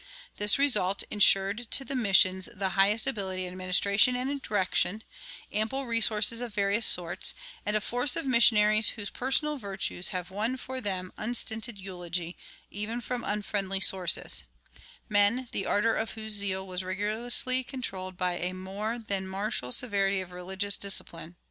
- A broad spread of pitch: No, average, 3.6 semitones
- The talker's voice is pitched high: Yes, high, 205 Hz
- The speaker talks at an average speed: Yes, average, 150 wpm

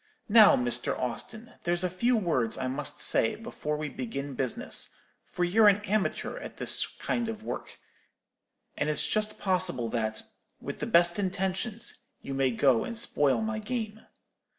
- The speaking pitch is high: No, medium, 180 Hz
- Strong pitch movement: Yes, wide, 8.1 semitones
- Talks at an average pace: Yes, average, 160 wpm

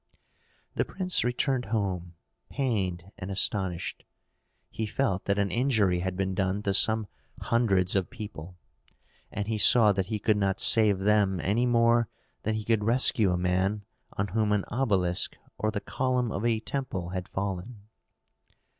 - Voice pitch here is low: Yes, low, 105 Hz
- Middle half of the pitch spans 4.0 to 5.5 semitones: No, average, 3.3 semitones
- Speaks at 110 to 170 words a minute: Yes, average, 155 wpm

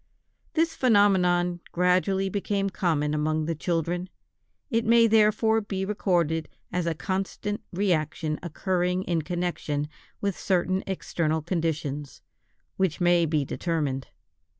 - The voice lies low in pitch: No, medium, 180 Hz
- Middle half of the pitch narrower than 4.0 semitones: Yes, average, 3.4 semitones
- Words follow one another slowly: Yes, slow, 115 wpm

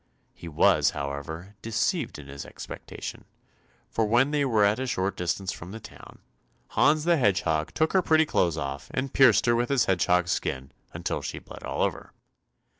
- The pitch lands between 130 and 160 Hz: No, low, 100 Hz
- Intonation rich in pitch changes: Yes, wide, 7.8 semitones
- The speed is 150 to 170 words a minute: No, average, 180 wpm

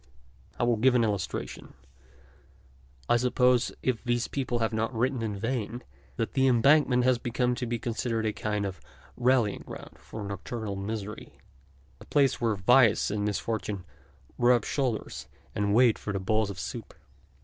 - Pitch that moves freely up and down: No, average, 2.9 semitones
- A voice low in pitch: Yes, low, 115 Hz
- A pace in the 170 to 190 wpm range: No, average, 155 wpm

